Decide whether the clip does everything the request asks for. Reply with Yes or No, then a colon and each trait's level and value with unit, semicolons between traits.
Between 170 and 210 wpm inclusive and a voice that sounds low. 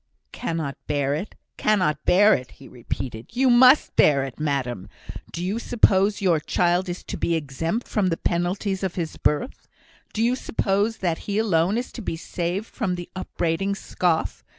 No: average, 175 wpm; medium, 180 Hz